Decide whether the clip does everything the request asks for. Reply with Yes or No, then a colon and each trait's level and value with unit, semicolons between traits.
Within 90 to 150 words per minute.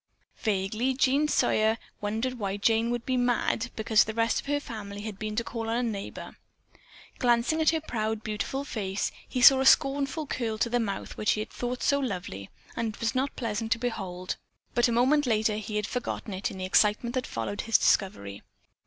No: fast, 205 wpm